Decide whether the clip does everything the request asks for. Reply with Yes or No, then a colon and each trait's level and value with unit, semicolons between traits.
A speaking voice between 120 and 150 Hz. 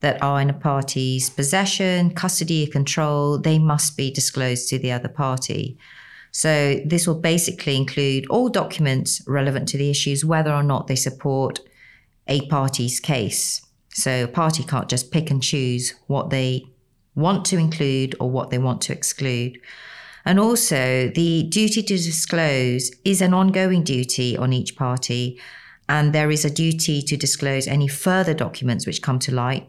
Yes: medium, 140 Hz